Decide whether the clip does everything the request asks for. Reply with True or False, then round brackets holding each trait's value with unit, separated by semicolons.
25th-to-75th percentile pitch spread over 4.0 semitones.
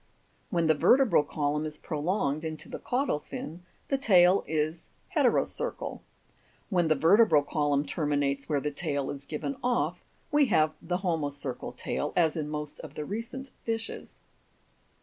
True (5.0 semitones)